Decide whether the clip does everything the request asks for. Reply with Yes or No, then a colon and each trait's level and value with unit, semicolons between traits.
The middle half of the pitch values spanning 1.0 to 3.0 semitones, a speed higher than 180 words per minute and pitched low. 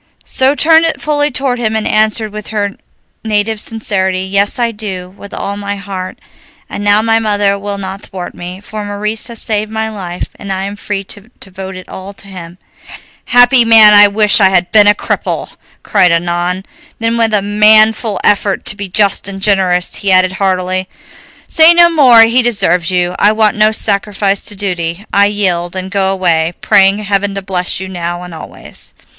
No: narrow, 2.4 semitones; average, 190 wpm; high, 200 Hz